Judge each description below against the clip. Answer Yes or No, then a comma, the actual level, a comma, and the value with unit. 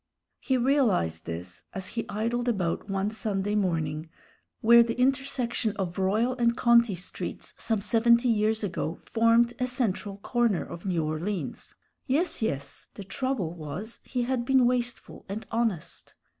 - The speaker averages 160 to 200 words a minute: No, average, 145 wpm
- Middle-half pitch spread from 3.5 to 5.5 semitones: Yes, average, 4.2 semitones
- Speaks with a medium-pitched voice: No, high, 220 Hz